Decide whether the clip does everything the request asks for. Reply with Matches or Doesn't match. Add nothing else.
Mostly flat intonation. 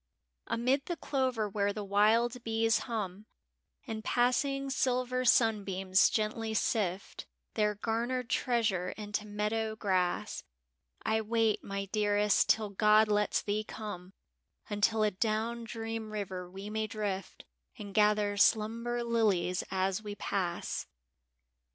Matches